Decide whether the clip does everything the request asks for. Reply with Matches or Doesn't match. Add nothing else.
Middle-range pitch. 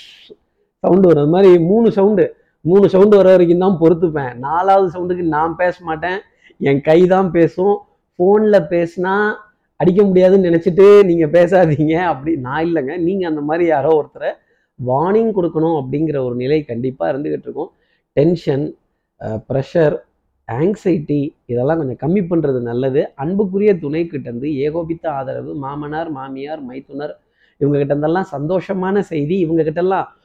Matches